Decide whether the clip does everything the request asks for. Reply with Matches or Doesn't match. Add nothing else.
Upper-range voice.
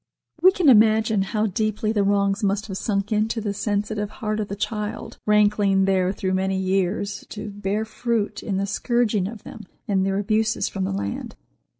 Matches